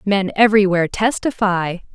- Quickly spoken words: No, slow, 95 wpm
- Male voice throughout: No, female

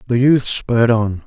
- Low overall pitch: Yes, low, 115 Hz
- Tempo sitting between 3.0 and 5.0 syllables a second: Yes, 4.7 syllables/s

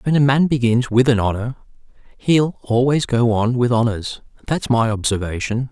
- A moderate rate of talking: Yes, average, 170 wpm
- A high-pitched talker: No, low, 120 Hz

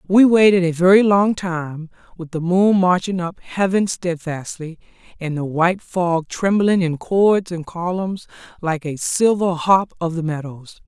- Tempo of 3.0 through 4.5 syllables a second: Yes, 4.2 syllables/s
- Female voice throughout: Yes, female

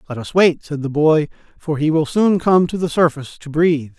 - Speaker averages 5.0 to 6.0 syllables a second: Yes, 5.5 syllables/s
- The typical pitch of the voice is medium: Yes, medium, 155 Hz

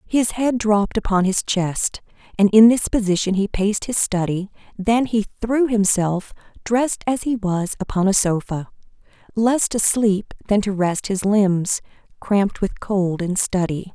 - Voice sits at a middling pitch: No, high, 205 Hz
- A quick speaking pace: No, average, 165 wpm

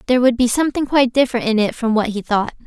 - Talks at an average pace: No, fast, 270 wpm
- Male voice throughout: No, female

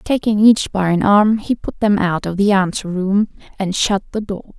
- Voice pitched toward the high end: Yes, high, 200 Hz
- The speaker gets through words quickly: Yes, fast, 210 wpm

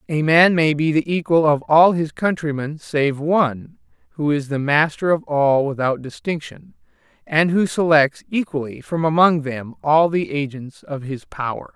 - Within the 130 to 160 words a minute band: No, average, 170 wpm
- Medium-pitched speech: Yes, medium, 155 Hz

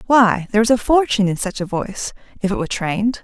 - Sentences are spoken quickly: Yes, fast, 240 wpm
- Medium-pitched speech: No, high, 210 Hz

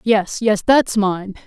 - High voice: Yes, high, 210 Hz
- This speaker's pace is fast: No, average, 165 wpm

